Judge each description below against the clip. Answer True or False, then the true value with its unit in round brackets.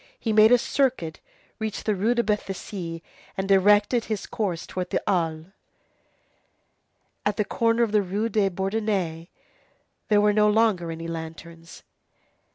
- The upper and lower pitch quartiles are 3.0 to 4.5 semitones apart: True (4.1 semitones)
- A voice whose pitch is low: False (205 Hz)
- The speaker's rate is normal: True (145 wpm)